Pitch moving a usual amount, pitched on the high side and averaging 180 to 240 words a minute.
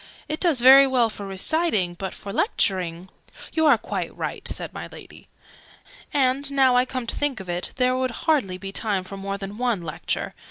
No: wide, 5.7 semitones; high, 235 Hz; average, 200 wpm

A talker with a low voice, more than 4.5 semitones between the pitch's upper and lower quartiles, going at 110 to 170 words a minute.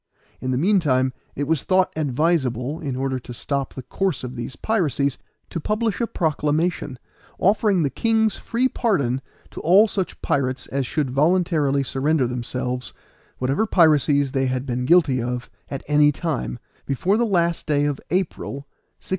No: medium, 145 Hz; wide, 5.4 semitones; average, 160 wpm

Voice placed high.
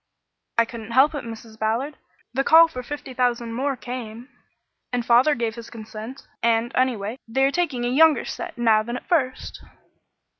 Yes: high, 245 Hz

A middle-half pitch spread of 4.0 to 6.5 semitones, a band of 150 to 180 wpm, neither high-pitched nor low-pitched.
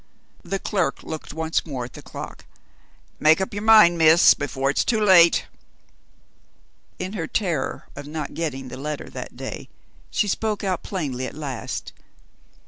Yes: average, 5.1 semitones; average, 155 wpm; medium, 160 Hz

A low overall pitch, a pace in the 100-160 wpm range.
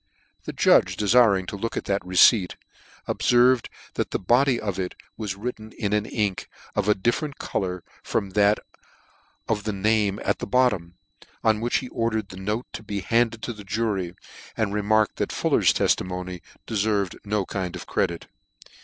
No: low, 105 Hz; average, 170 wpm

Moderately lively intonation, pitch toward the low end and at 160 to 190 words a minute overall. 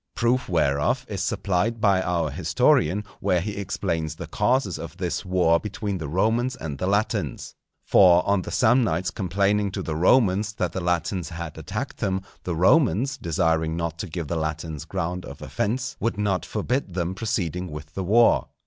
Yes: average, 4.0 semitones; very low, 95 Hz; average, 175 wpm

